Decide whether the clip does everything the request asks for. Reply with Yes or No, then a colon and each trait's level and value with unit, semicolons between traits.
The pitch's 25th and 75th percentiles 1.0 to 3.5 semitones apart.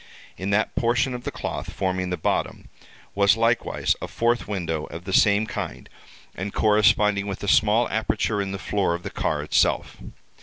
Yes: average, 2.8 semitones